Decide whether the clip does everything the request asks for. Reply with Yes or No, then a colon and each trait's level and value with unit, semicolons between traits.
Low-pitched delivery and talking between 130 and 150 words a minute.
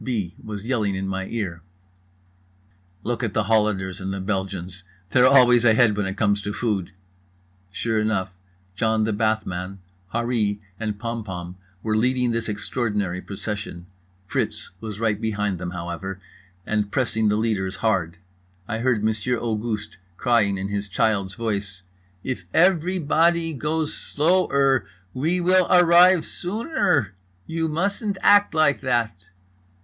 Yes: low, 110 Hz; average, 145 wpm